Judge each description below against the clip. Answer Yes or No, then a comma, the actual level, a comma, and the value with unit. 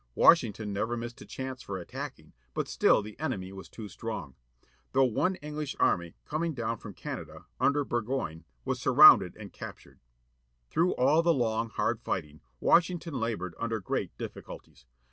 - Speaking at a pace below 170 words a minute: Yes, average, 155 wpm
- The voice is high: No, low, 115 Hz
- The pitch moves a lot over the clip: Yes, wide, 5.7 semitones